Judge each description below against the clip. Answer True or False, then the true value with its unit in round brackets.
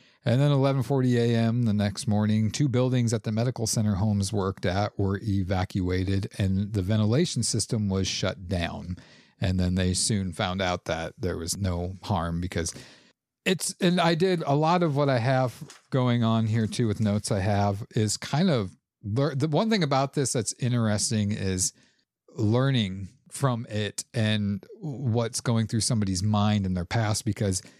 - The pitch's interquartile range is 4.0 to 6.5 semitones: True (4.3 semitones)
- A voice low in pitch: True (110 Hz)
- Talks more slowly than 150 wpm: False (175 wpm)